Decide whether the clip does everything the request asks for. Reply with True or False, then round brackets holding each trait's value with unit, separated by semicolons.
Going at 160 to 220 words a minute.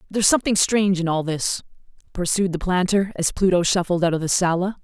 True (200 wpm)